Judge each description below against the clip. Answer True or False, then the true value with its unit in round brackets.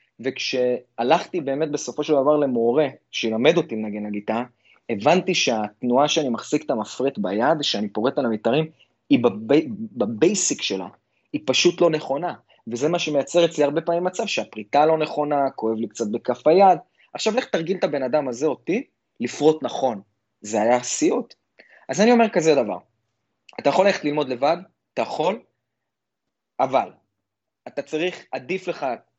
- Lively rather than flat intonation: True (6.2 semitones)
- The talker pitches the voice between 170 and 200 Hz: False (150 Hz)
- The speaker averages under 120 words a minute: False (150 wpm)